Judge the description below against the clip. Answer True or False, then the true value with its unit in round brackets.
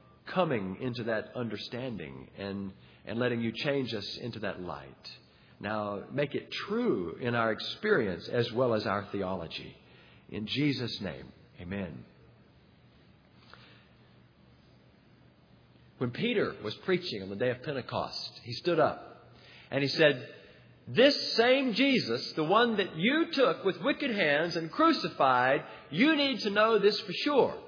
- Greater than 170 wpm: False (140 wpm)